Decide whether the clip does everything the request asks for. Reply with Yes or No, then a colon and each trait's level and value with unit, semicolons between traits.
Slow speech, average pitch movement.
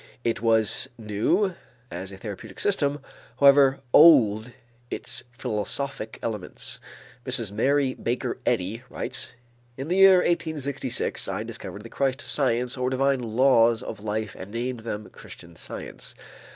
Yes: slow, 130 wpm; average, 4.2 semitones